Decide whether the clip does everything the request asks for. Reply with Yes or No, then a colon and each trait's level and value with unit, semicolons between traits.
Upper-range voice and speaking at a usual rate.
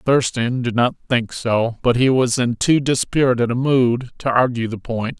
No: low, 125 Hz; average, 195 wpm